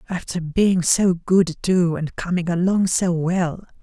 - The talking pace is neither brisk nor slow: Yes, average, 155 wpm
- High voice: No, medium, 175 Hz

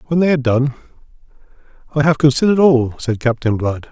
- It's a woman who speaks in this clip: No, male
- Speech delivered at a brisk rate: No, average, 170 wpm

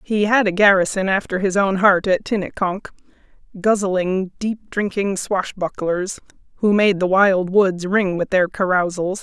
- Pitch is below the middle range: No, high, 190 Hz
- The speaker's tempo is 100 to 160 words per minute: Yes, average, 150 wpm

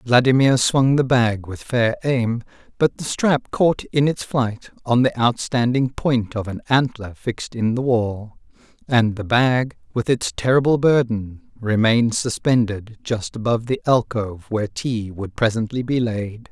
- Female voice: No, male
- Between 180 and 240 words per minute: No, average, 160 wpm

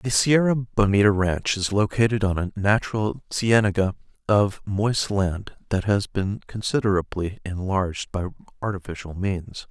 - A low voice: Yes, low, 100 Hz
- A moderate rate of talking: No, slow, 130 wpm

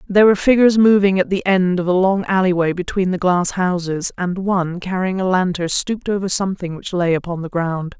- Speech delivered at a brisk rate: Yes, fast, 210 wpm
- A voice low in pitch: No, medium, 185 Hz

